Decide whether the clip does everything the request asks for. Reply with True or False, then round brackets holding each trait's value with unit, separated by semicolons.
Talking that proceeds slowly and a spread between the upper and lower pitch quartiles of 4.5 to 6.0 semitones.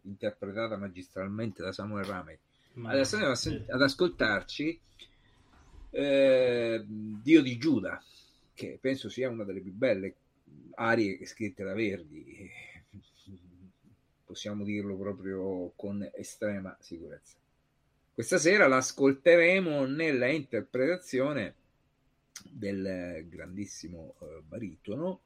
True (95 wpm; 5.4 semitones)